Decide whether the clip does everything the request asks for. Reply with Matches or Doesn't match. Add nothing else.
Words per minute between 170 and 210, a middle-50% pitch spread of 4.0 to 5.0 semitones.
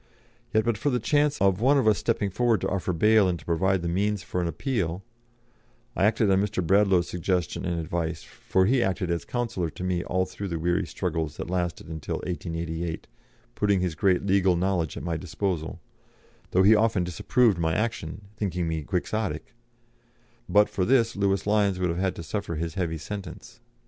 Doesn't match